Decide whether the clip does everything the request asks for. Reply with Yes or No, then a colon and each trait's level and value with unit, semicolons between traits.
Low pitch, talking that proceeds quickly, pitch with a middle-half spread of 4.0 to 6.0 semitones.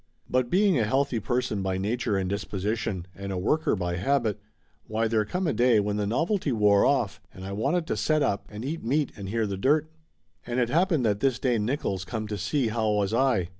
Yes: low, 115 Hz; fast, 225 wpm; average, 5.1 semitones